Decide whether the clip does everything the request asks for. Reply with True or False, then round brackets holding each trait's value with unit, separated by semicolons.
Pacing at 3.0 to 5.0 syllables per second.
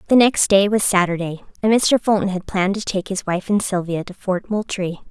False (5.4 syllables/s)